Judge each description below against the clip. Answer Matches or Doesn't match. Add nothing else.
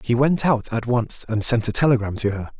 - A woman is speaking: Doesn't match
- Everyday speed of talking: Doesn't match